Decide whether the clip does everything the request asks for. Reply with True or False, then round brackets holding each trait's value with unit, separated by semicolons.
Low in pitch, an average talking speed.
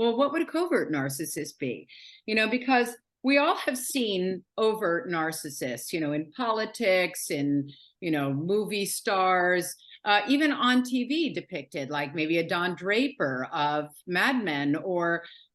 False (185 Hz; 150 wpm)